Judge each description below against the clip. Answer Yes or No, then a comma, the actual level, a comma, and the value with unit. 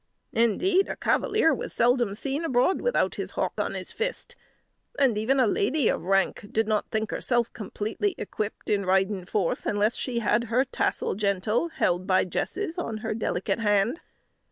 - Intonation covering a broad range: No, average, 4.8 semitones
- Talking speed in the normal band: Yes, average, 170 wpm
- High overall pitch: Yes, high, 225 Hz